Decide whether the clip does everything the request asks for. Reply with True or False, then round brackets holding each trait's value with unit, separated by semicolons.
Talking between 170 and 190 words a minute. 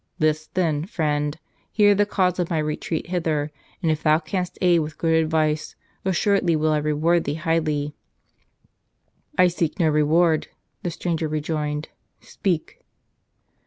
False (145 wpm)